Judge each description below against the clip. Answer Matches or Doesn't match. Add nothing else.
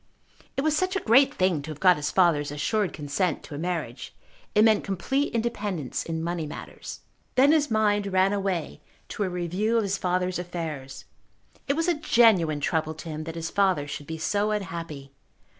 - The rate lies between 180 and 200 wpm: Matches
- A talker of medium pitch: Matches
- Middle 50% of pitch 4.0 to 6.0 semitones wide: Matches